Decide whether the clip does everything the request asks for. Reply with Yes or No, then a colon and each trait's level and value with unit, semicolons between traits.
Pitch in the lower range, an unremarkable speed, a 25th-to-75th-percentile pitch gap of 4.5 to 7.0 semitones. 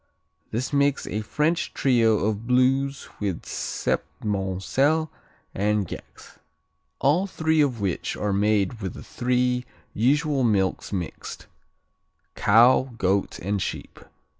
No: low, 115 Hz; slow, 115 wpm; average, 5.2 semitones